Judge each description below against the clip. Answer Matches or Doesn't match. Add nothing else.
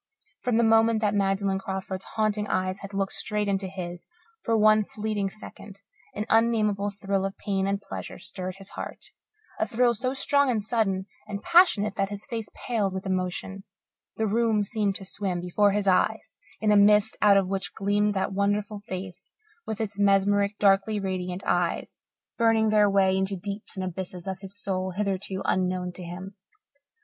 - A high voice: Matches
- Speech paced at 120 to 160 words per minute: Doesn't match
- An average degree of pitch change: Doesn't match